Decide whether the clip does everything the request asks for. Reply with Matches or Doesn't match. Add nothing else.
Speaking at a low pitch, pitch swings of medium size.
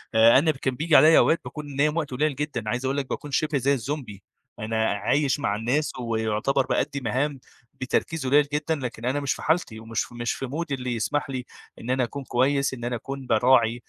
Matches